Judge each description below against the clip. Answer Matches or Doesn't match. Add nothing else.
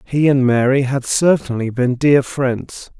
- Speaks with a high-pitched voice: Doesn't match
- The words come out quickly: Doesn't match